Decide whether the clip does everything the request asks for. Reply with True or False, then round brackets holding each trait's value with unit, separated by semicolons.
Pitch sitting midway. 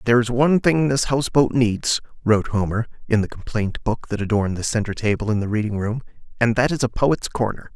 False (115 Hz)